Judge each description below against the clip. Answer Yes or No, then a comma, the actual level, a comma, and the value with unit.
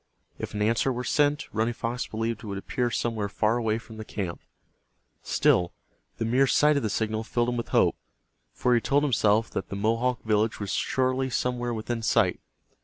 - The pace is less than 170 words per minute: No, average, 190 wpm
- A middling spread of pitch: No, narrow, 2.3 semitones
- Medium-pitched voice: No, low, 115 Hz